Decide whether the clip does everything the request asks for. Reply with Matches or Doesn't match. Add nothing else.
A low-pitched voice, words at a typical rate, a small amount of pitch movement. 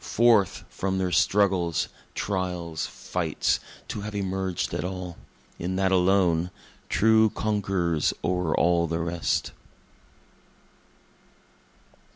Doesn't match